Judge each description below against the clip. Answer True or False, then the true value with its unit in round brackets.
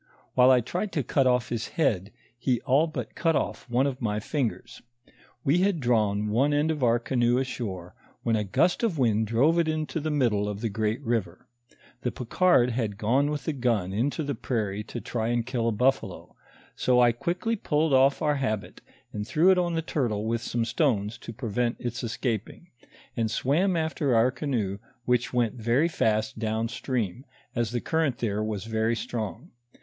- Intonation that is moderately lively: True (4.4 semitones)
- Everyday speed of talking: True (190 wpm)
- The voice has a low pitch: True (120 Hz)